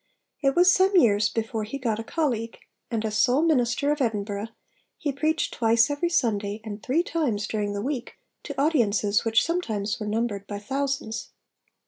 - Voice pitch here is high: Yes, high, 230 Hz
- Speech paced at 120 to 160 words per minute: No, average, 170 wpm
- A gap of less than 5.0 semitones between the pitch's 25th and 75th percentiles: No, average, 5.3 semitones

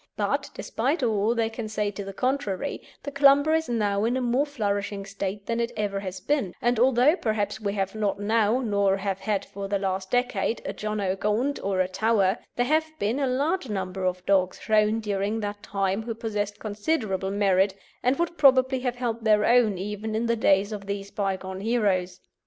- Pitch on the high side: Yes, high, 210 Hz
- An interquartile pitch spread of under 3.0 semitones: No, average, 3.5 semitones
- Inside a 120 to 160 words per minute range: No, average, 200 wpm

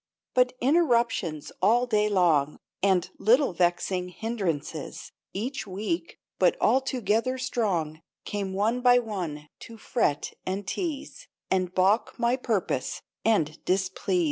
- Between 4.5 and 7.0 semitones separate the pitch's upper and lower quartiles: Yes, average, 5.2 semitones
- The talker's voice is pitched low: No, high, 205 Hz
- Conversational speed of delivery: No, slow, 120 wpm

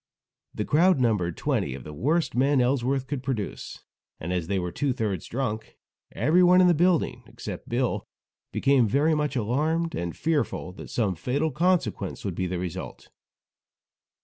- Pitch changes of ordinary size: No, wide, 7.8 semitones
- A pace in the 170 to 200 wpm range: No, average, 160 wpm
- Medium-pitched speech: No, low, 130 Hz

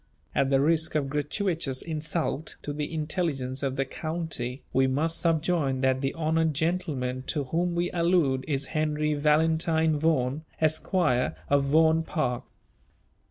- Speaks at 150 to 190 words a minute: No, average, 140 wpm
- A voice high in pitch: No, medium, 155 Hz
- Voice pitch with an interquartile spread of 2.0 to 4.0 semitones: Yes, average, 3.1 semitones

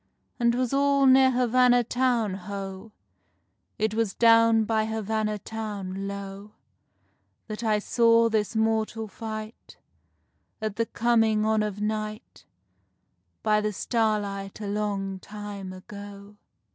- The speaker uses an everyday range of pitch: No, narrow, 2.0 semitones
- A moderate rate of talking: No, slow, 120 wpm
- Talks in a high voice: Yes, high, 215 Hz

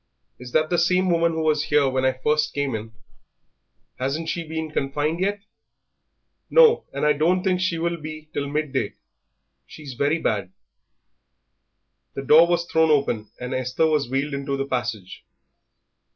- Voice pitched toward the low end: No, medium, 150 Hz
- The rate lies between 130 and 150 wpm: No, average, 160 wpm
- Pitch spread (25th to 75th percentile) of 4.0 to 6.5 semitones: No, average, 3.6 semitones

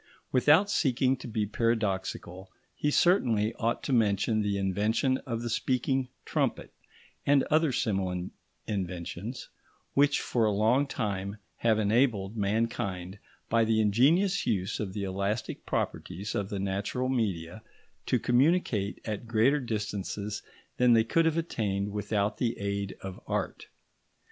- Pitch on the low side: Yes, low, 110 Hz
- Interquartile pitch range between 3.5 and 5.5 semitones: Yes, average, 4.0 semitones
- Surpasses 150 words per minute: No, slow, 135 wpm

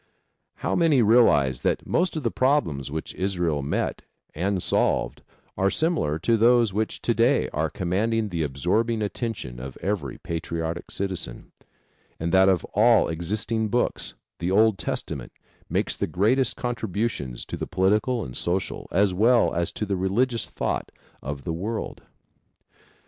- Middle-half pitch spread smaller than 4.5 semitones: No, wide, 5.5 semitones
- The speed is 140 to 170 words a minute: Yes, average, 150 wpm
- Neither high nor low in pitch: No, low, 100 Hz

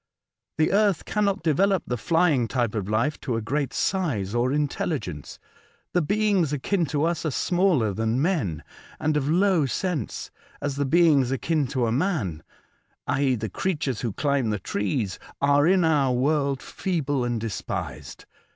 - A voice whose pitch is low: No, medium, 145 Hz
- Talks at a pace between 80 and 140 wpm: No, average, 155 wpm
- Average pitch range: No, wide, 5.9 semitones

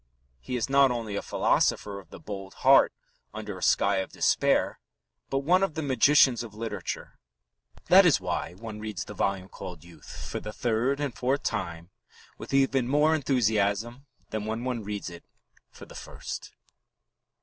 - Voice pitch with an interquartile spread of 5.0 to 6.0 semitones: Yes, average, 5.3 semitones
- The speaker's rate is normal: Yes, average, 170 wpm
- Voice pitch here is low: Yes, low, 110 Hz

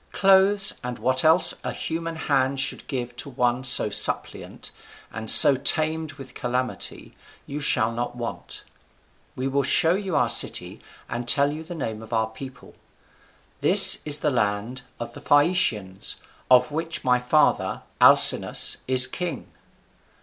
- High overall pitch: No, low, 130 Hz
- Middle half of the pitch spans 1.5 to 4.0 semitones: No, average, 4.4 semitones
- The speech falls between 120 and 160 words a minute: Yes, average, 150 wpm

